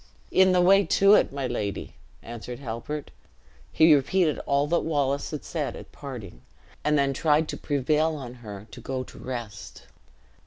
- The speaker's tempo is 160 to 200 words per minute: Yes, average, 165 wpm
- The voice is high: No, medium, 140 Hz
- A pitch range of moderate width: Yes, average, 4.2 semitones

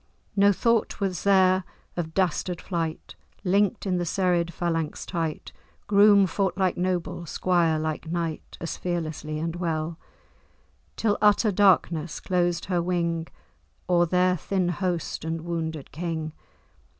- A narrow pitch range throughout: Yes, narrow, 2.3 semitones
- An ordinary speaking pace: No, slow, 130 wpm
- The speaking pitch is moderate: Yes, medium, 175 Hz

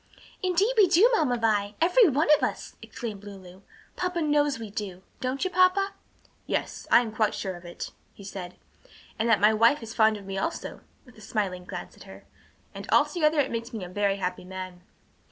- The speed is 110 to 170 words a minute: No, average, 200 wpm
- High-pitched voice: Yes, high, 225 Hz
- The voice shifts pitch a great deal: Yes, wide, 7.5 semitones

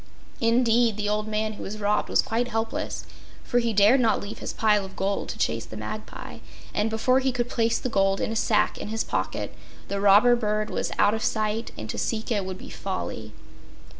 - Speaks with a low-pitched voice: No, high, 215 Hz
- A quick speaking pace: Yes, fast, 215 wpm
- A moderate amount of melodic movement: No, narrow, 2.2 semitones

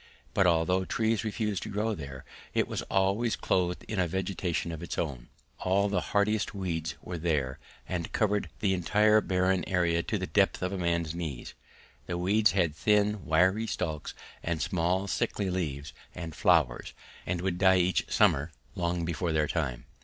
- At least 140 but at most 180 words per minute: Yes, average, 170 wpm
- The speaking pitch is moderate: No, very low, 90 Hz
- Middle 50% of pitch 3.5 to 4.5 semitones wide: No, average, 3.1 semitones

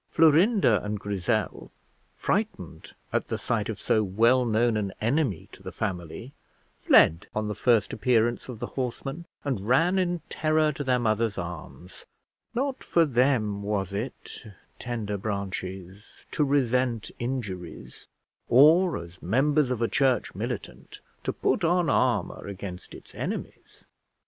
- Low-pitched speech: Yes, low, 115 Hz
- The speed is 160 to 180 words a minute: No, average, 140 wpm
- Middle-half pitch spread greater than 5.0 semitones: Yes, wide, 5.6 semitones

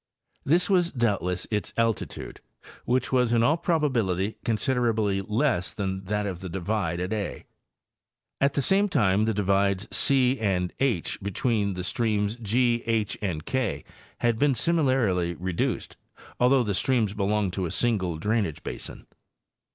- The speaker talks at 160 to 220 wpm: No, average, 145 wpm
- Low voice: Yes, low, 110 Hz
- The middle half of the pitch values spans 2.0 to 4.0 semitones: No, average, 4.5 semitones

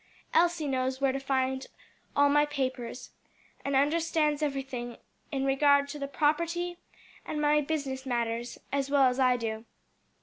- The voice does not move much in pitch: Yes, narrow, 2.2 semitones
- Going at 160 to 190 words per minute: No, average, 145 wpm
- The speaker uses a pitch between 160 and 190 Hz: No, very high, 275 Hz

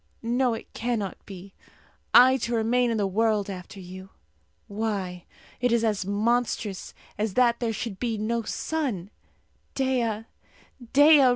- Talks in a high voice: Yes, high, 225 Hz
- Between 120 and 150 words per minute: Yes, slow, 135 wpm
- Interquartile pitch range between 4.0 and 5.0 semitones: No, average, 3.3 semitones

